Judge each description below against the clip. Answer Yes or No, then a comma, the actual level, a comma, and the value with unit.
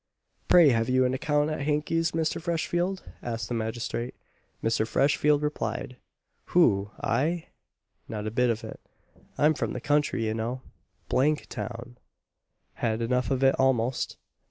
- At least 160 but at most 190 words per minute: No, average, 150 wpm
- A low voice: Yes, low, 130 Hz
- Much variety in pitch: No, average, 4.6 semitones